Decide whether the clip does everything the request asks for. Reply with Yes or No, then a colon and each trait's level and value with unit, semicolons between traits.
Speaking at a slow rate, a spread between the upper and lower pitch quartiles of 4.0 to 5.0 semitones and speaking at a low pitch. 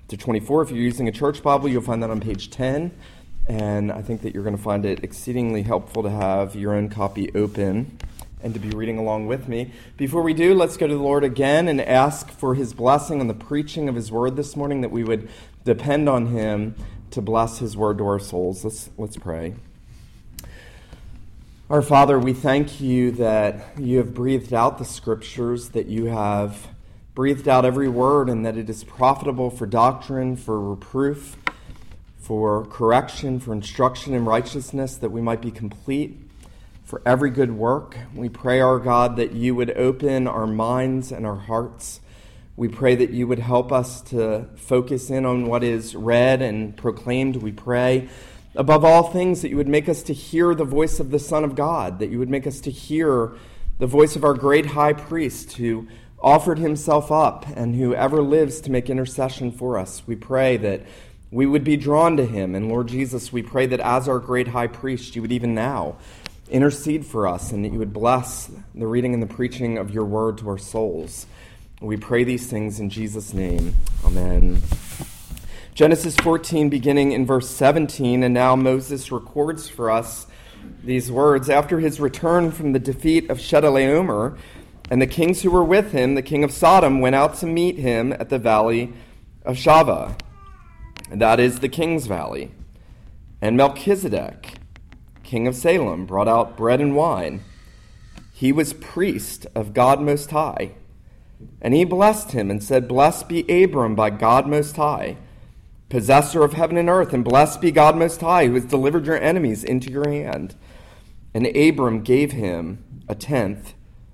No: average, 185 wpm; average, 4.3 semitones; low, 125 Hz